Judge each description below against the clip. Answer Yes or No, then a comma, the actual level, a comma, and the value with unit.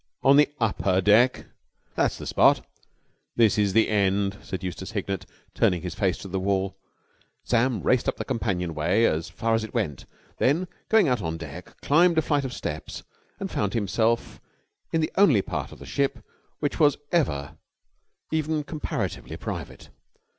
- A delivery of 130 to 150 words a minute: No, average, 170 wpm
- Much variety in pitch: Yes, wide, 6.6 semitones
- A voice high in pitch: No, low, 110 Hz